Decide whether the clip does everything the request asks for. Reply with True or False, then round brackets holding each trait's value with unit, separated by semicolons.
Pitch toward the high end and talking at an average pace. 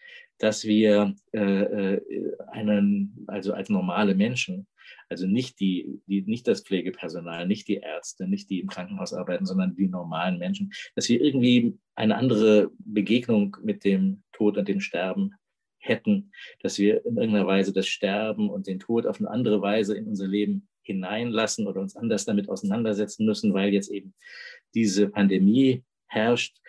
False (110 Hz; 155 wpm)